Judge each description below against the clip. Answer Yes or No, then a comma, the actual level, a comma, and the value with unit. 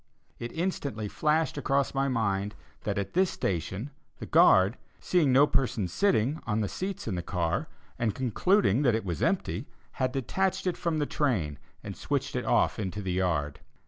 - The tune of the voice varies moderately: No, wide, 7.0 semitones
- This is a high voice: No, low, 120 Hz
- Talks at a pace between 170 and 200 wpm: Yes, average, 175 wpm